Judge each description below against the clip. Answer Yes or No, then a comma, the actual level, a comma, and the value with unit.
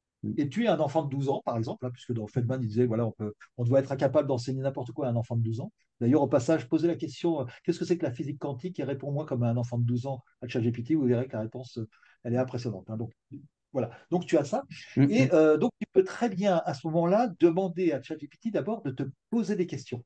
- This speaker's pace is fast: Yes, fast, 270 wpm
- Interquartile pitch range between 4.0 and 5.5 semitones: Yes, average, 4.9 semitones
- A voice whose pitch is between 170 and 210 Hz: No, medium, 140 Hz